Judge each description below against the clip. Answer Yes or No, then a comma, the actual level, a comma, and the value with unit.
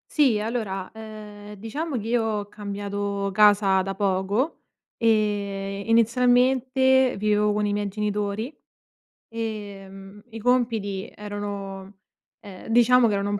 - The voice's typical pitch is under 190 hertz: No, high, 210 Hz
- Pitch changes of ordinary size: No, narrow, 2.2 semitones